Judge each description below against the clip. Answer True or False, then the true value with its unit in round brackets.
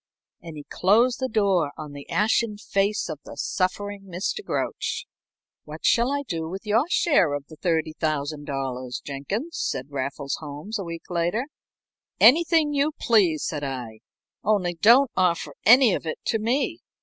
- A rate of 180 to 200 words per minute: False (155 wpm)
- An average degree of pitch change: False (7.2 semitones)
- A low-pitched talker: False (185 Hz)